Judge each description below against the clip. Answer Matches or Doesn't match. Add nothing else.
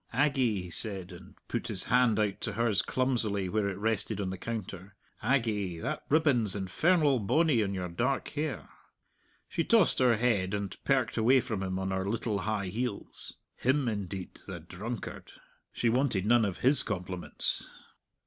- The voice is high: Doesn't match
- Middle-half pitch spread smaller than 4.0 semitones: Doesn't match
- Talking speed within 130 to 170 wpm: Matches